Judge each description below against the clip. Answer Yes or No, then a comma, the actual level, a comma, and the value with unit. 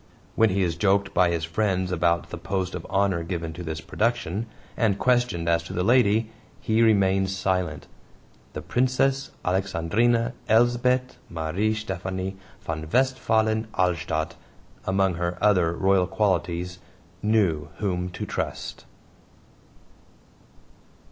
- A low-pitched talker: Yes, very low, 95 Hz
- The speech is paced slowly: Yes, slow, 120 wpm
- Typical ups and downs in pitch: Yes, average, 4.2 semitones